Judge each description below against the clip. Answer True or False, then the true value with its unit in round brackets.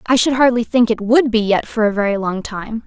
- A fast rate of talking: True (270 wpm)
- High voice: True (225 Hz)